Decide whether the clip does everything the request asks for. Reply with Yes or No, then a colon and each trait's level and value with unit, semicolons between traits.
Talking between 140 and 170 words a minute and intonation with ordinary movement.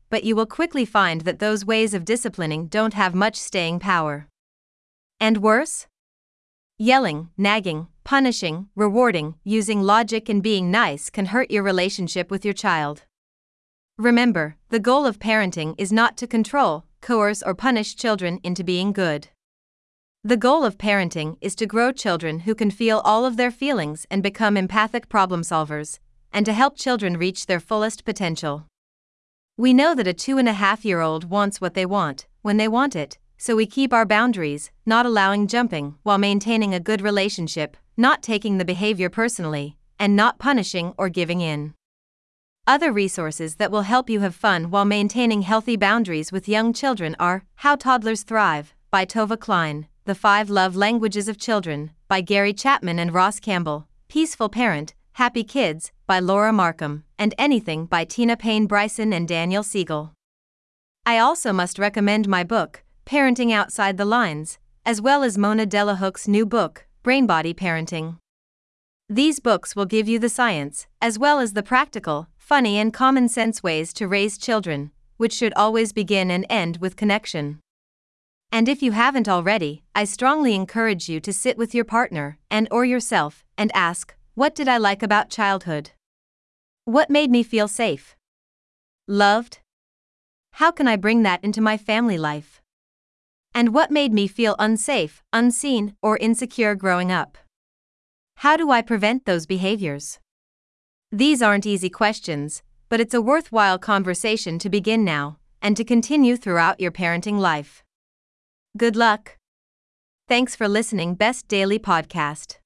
Yes: average, 160 wpm; average, 4.4 semitones